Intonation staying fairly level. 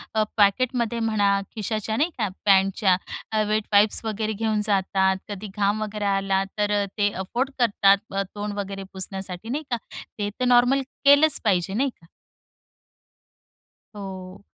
Yes: narrow, 2.3 semitones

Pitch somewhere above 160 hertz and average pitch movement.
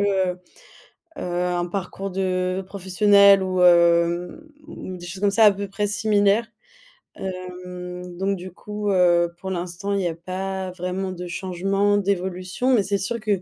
No: medium, 185 Hz; narrow, 1.9 semitones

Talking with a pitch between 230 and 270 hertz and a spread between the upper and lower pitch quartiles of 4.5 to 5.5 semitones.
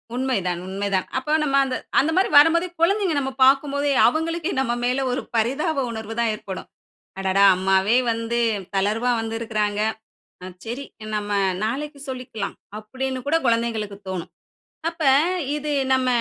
Yes: high, 245 Hz; average, 5.1 semitones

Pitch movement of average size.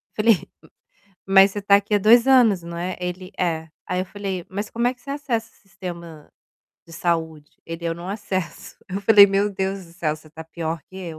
Yes: average, 3.4 semitones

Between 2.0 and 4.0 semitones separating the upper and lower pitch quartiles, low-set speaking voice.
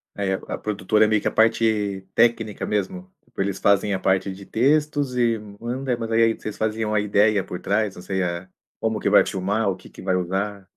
Yes: average, 2.7 semitones; low, 105 Hz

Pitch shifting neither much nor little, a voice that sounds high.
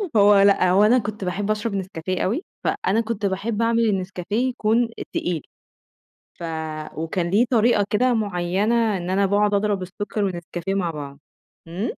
Yes: average, 3.1 semitones; high, 200 Hz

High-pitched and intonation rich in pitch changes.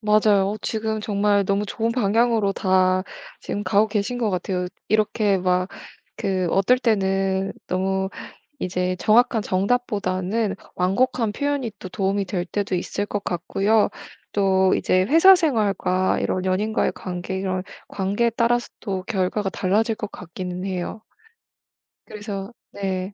No: high, 200 Hz; average, 2.7 semitones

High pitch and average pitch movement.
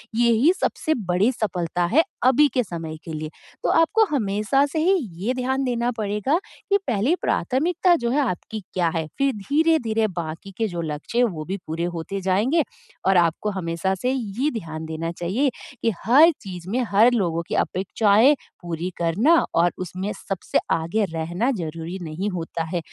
No: high, 200 Hz; wide, 6.9 semitones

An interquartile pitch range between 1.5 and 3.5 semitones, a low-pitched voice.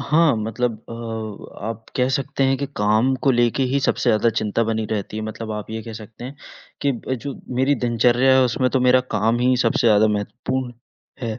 Yes: average, 3.1 semitones; low, 120 Hz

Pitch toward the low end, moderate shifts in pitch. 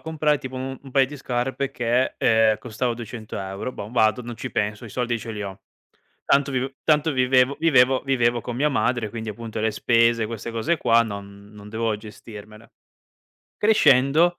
Yes: low, 120 Hz; average, 3.3 semitones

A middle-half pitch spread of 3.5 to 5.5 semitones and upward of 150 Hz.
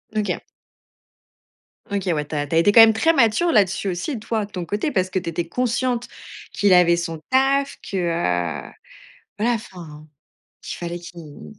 Yes: average, 5.1 semitones; medium, 185 Hz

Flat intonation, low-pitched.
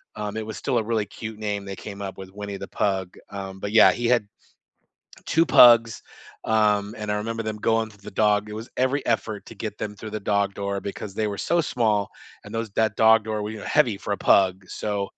Yes: narrow, 1.7 semitones; low, 105 Hz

